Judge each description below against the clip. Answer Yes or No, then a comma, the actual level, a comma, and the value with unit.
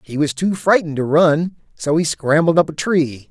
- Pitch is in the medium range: Yes, medium, 160 Hz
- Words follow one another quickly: Yes, fast, 220 wpm